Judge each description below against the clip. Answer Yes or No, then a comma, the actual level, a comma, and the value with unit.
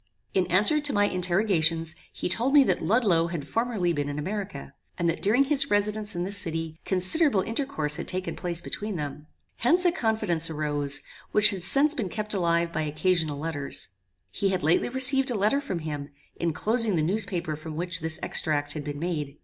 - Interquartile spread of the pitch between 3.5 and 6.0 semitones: Yes, average, 5.2 semitones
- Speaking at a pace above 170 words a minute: Yes, average, 190 wpm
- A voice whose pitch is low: No, medium, 180 Hz